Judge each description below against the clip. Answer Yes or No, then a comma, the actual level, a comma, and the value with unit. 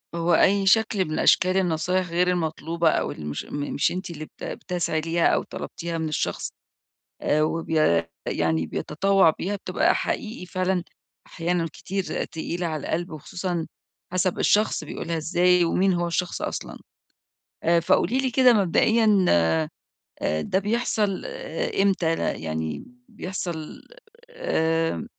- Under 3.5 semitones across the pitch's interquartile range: Yes, average, 3.0 semitones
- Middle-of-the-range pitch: Yes, medium, 175 Hz